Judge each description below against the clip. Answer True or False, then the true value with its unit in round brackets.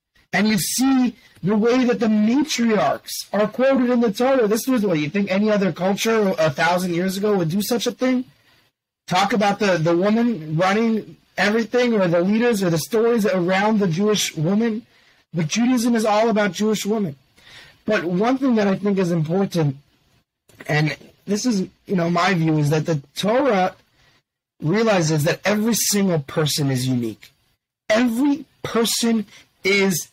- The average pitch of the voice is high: True (200 Hz)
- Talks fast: False (165 wpm)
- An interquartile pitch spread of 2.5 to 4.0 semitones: False (5.3 semitones)